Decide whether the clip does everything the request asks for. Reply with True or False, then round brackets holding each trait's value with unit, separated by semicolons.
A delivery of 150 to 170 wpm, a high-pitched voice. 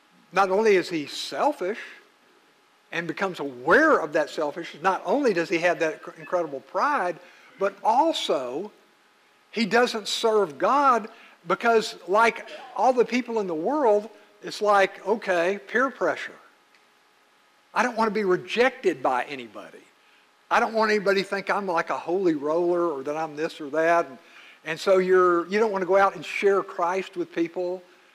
True (165 wpm; 195 Hz)